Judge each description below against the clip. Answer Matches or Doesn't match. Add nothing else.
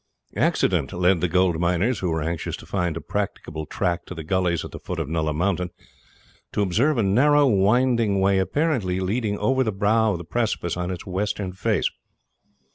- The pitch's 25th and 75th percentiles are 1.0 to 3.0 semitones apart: Doesn't match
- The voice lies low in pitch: Matches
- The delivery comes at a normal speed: Matches